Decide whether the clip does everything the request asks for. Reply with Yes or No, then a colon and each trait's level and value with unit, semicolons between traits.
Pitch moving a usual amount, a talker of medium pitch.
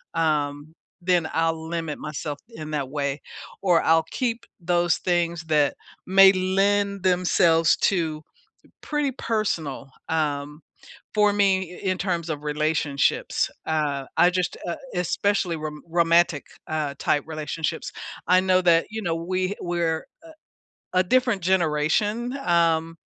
Yes: average, 3.2 semitones; medium, 170 Hz